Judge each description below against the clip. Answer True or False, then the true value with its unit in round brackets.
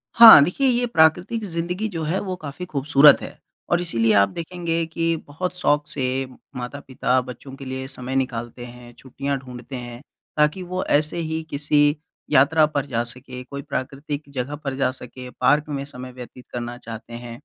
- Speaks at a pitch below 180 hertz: True (140 Hz)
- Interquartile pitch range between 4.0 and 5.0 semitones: True (4.3 semitones)